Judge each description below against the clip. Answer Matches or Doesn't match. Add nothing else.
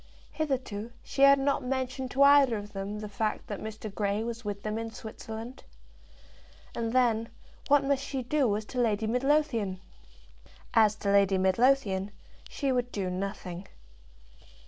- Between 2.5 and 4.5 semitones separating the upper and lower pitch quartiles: Matches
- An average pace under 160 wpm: Matches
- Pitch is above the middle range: Matches